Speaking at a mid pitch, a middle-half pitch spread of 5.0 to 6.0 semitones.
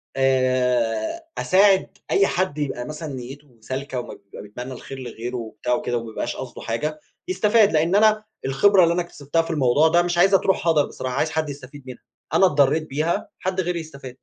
Yes: medium, 145 Hz; average, 5.3 semitones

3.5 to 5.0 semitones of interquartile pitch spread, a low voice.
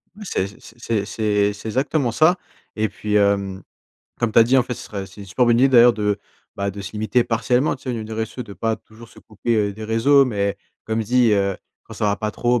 No: average, 2.9 semitones; low, 110 Hz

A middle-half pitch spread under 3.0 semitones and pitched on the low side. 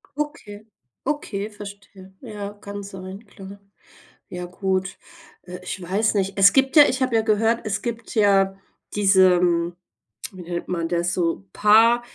No: narrow, 2.6 semitones; high, 200 Hz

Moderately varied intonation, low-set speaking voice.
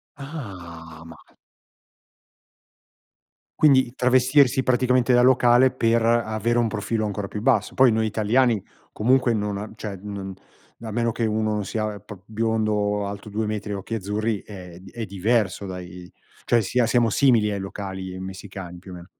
Yes: average, 3.2 semitones; low, 110 Hz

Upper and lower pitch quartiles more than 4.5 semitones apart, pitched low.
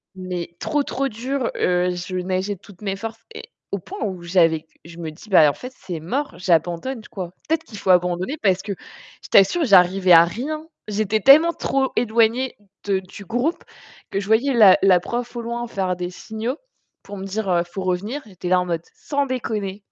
No: average, 4.9 semitones; high, 200 Hz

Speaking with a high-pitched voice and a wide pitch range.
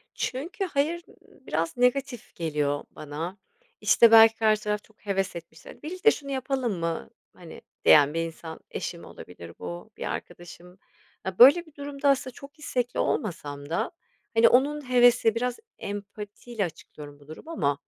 Yes: high, 220 Hz; wide, 8.1 semitones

